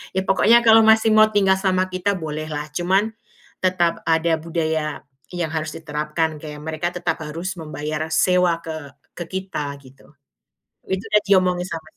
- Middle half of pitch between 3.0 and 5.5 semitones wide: Yes, average, 3.3 semitones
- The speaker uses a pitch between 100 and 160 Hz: No, medium, 170 Hz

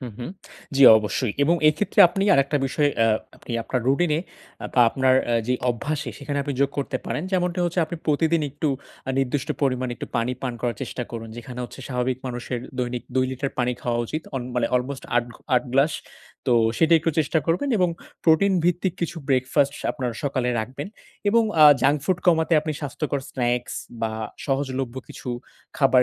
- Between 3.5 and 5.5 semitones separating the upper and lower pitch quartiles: Yes, average, 3.8 semitones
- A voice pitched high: No, low, 135 Hz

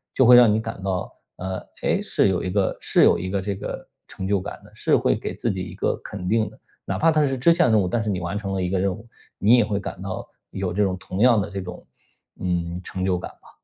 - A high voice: No, low, 100 Hz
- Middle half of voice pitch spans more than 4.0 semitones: No, average, 3.1 semitones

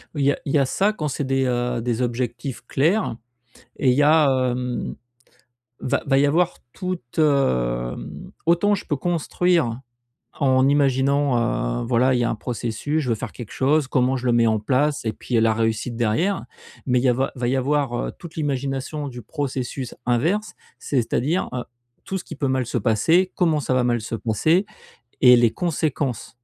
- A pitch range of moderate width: Yes, average, 3.6 semitones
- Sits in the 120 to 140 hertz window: Yes, low, 130 Hz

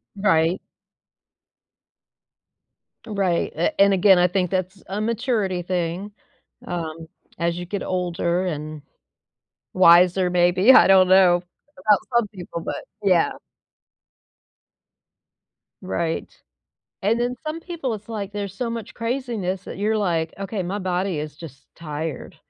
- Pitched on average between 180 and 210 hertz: Yes, medium, 185 Hz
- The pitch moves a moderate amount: Yes, average, 3.2 semitones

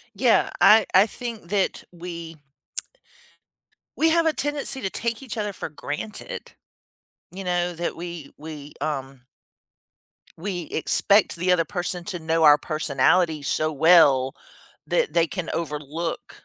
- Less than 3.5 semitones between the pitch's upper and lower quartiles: No, average, 4.3 semitones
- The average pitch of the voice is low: No, medium, 170 Hz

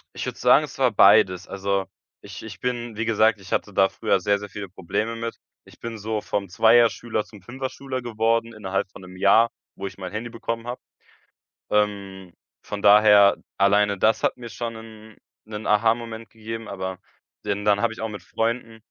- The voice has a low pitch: Yes, low, 110 Hz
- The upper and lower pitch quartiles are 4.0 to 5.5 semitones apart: No, narrow, 2.5 semitones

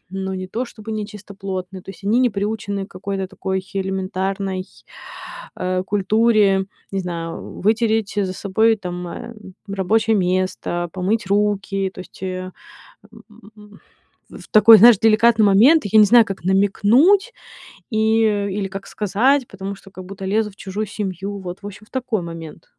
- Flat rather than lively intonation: Yes, narrow, 2.3 semitones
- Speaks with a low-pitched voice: No, high, 200 Hz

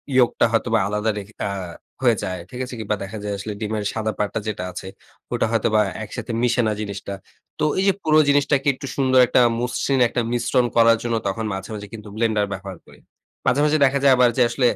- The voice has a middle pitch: No, low, 115 Hz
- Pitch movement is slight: No, average, 3.2 semitones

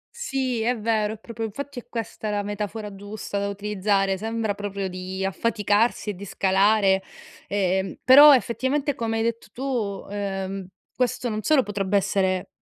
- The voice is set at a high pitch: Yes, high, 210 Hz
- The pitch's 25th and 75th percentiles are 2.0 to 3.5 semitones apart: Yes, average, 2.8 semitones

